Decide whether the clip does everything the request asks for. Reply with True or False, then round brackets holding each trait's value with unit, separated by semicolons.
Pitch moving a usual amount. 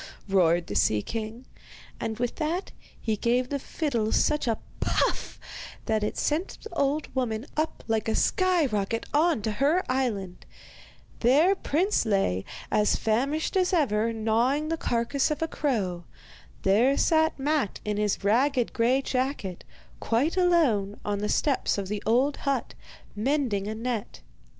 False (5.8 semitones)